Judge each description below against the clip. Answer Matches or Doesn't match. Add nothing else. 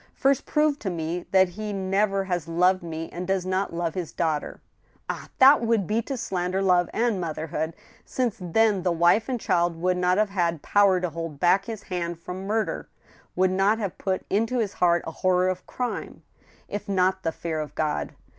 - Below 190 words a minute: Doesn't match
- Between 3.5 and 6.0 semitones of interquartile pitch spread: Doesn't match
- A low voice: Doesn't match